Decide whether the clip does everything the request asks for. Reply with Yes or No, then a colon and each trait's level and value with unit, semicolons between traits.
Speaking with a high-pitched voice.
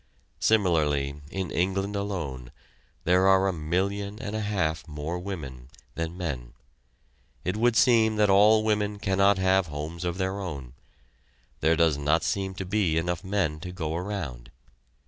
No: very low, 90 Hz